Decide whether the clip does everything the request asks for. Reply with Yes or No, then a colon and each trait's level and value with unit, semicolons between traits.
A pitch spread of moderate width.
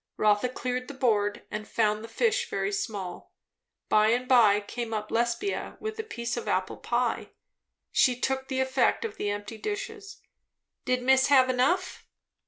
Yes: average, 3.8 semitones